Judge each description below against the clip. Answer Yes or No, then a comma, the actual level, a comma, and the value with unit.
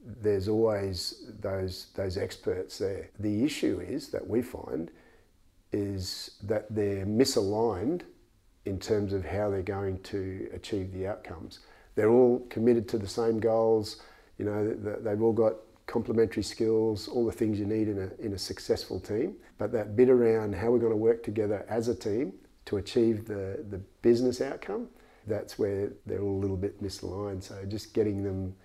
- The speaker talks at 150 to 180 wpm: Yes, average, 170 wpm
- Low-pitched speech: Yes, low, 105 Hz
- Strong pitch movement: No, narrow, 2.5 semitones